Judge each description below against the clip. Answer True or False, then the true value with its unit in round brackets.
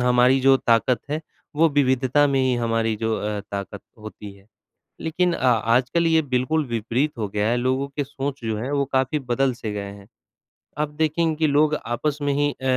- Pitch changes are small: False (4.2 semitones)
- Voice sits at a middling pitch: False (130 Hz)